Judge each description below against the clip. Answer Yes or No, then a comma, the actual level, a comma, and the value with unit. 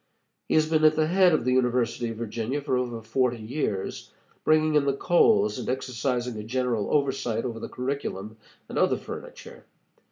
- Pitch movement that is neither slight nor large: Yes, average, 4.2 semitones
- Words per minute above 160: Yes, average, 180 wpm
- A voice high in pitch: No, low, 125 Hz